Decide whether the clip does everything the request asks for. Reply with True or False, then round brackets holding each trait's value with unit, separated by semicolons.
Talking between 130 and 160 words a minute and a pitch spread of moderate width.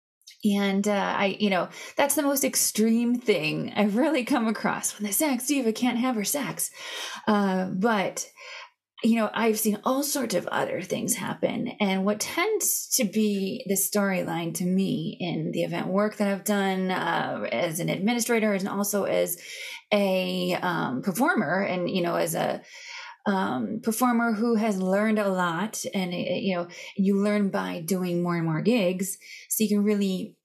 False (175 wpm; 3.9 semitones)